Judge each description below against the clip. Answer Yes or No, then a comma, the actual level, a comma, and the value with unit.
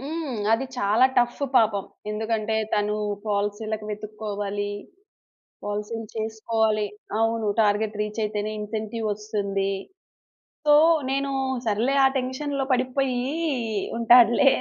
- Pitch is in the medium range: No, high, 220 Hz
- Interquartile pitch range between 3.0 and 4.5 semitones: No, narrow, 2.5 semitones